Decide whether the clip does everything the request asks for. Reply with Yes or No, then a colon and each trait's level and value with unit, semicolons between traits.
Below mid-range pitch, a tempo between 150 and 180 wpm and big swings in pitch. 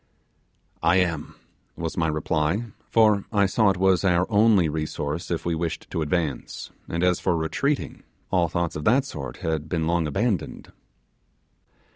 No: very low, 85 Hz; average, 155 wpm; average, 3.5 semitones